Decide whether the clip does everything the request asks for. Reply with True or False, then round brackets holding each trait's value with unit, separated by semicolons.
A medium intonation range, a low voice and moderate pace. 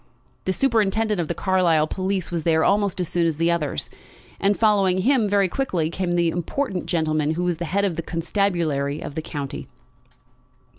False (3.6 semitones; 175 Hz; 185 wpm)